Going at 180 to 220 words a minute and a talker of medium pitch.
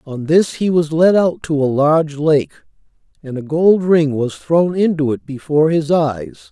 Yes: average, 195 wpm; medium, 155 Hz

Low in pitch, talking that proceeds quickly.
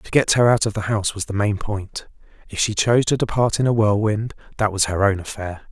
Yes: low, 105 Hz; fast, 250 wpm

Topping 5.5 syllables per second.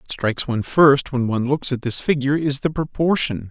Yes: 5.8 syllables/s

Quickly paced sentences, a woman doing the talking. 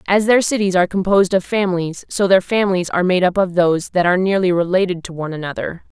Yes: fast, 220 wpm; female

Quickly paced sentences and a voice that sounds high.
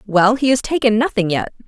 Yes: fast, 215 wpm; high, 225 Hz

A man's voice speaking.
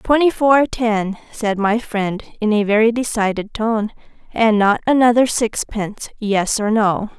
No: female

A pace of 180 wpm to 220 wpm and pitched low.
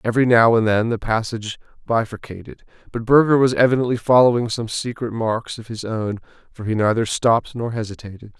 No: average, 170 wpm; low, 115 Hz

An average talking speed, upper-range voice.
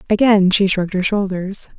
Yes: average, 170 wpm; high, 195 Hz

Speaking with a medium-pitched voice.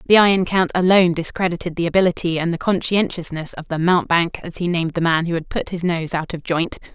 Yes: medium, 170 Hz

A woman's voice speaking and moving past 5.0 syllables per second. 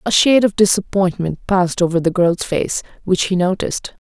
Yes: female; 5.5 syllables/s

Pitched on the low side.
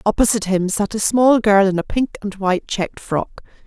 No: high, 205 Hz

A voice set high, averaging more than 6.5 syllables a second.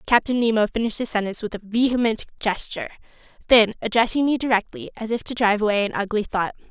Yes: high, 225 Hz; 6.9 syllables/s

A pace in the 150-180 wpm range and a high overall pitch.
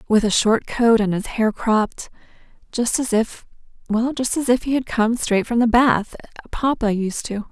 No: average, 200 wpm; high, 230 Hz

